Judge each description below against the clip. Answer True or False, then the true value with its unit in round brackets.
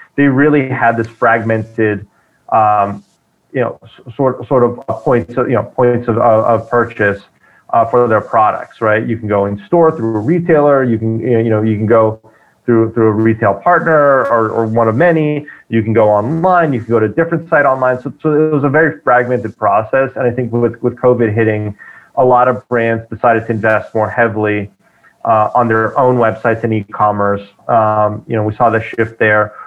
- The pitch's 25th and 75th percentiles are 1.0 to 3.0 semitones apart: True (2.5 semitones)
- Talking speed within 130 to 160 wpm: False (200 wpm)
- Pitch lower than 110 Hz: False (115 Hz)